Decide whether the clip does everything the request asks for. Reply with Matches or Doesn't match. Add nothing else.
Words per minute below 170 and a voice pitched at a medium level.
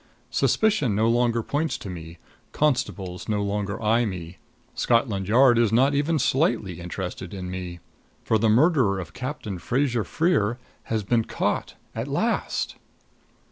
Doesn't match